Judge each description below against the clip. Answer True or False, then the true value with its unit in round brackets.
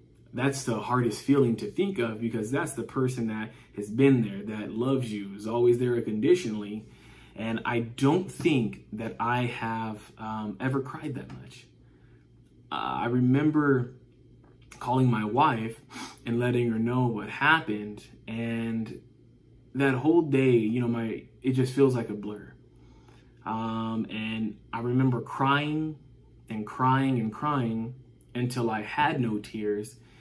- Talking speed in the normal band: True (145 wpm)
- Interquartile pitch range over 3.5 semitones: False (2.8 semitones)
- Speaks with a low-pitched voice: True (120 Hz)